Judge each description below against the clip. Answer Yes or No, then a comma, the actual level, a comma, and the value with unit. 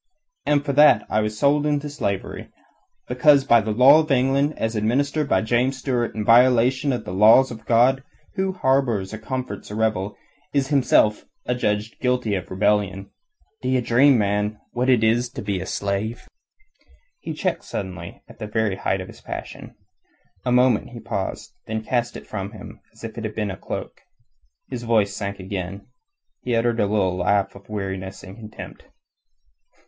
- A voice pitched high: No, low, 115 Hz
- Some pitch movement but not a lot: Yes, average, 4.1 semitones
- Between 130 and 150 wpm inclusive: No, average, 175 wpm